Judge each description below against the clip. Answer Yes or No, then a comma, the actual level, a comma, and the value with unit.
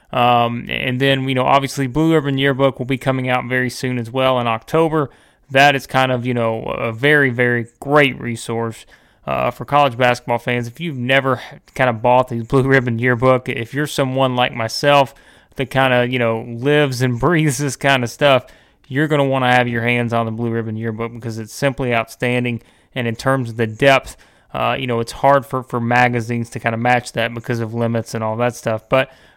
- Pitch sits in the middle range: No, low, 125 Hz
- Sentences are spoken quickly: Yes, fast, 215 wpm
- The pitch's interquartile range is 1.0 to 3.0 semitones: Yes, narrow, 2.6 semitones